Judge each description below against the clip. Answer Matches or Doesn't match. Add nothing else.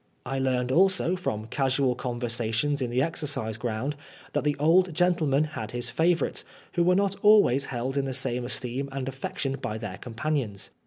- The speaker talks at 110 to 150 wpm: Doesn't match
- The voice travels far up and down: Doesn't match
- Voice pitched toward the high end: Doesn't match